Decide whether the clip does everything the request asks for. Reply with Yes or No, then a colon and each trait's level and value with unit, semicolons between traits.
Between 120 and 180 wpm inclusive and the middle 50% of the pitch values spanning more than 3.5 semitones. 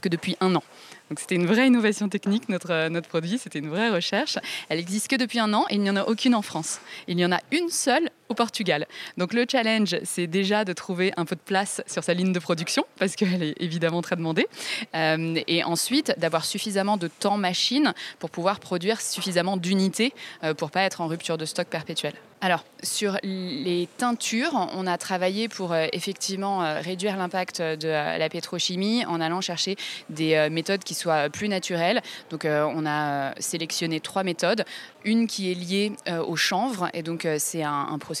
No: average, 190 wpm; average, 3.9 semitones